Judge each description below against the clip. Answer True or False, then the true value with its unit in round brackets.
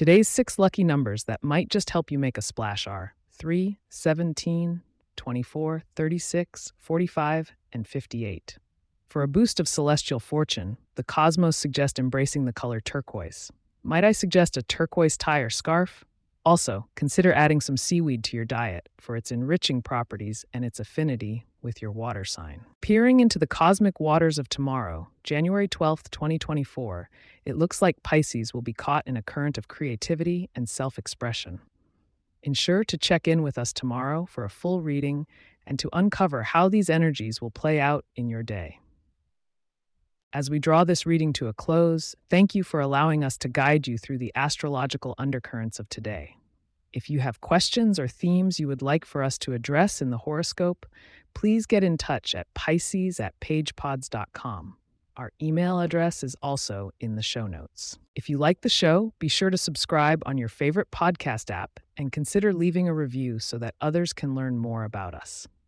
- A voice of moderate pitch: True (145 Hz)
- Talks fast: False (175 wpm)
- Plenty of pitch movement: True (6.1 semitones)